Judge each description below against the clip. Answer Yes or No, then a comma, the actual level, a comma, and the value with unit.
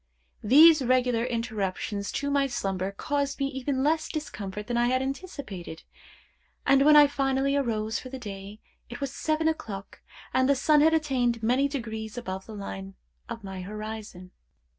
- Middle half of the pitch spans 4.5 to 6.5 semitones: Yes, average, 5.0 semitones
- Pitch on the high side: Yes, high, 245 Hz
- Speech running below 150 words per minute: No, average, 160 wpm